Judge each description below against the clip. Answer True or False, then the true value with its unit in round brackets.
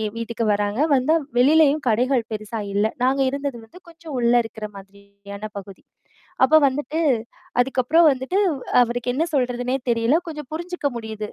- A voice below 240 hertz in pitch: False (245 Hz)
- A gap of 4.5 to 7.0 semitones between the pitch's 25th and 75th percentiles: True (4.8 semitones)